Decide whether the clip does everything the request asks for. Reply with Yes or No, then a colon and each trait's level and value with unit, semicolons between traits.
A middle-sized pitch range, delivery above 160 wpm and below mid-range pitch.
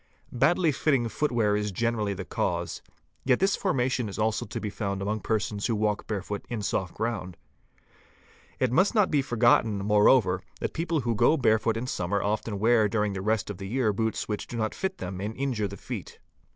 Yes: average, 3.4 semitones; average, 200 wpm; low, 110 Hz